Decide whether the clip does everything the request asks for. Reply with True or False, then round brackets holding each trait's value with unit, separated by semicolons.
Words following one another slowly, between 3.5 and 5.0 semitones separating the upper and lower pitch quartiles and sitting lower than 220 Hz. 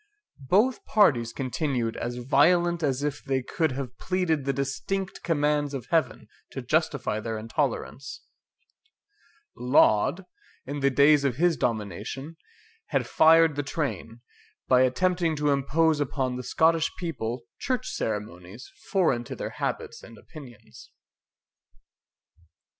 True (125 wpm; 4.6 semitones; 140 Hz)